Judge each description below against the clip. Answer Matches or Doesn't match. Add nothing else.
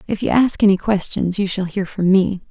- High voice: Matches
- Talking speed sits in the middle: Doesn't match